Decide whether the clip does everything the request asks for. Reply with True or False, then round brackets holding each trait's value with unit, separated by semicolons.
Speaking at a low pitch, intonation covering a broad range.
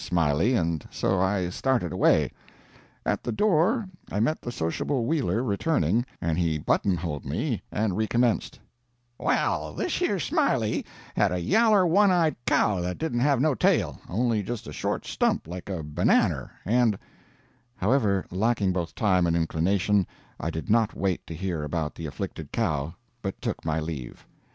True (95 Hz; 6.3 semitones)